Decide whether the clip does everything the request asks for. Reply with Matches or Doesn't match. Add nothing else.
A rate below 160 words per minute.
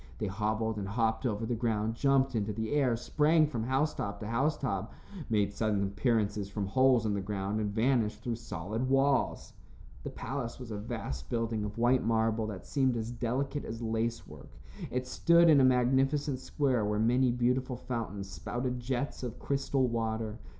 Doesn't match